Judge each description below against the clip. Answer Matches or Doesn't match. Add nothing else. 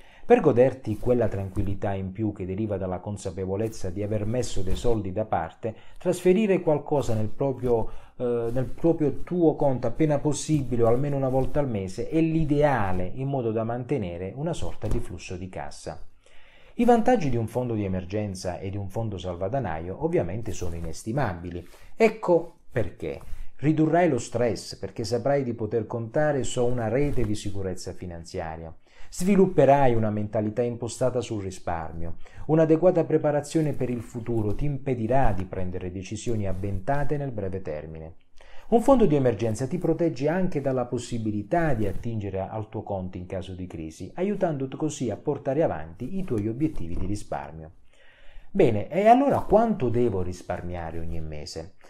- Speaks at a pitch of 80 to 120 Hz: Matches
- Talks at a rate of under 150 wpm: Doesn't match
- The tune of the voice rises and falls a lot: Matches